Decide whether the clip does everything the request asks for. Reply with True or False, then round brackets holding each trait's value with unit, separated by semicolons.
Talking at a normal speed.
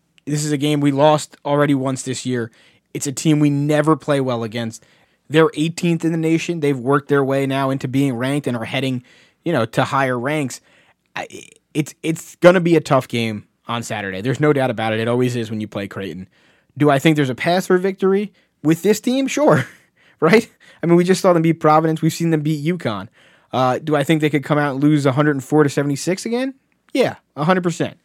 False (220 wpm)